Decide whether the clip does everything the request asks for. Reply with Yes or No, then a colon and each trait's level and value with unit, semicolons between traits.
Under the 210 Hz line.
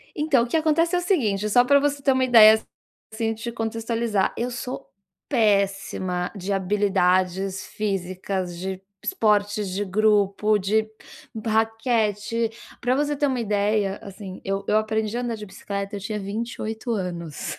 No: high, 215 Hz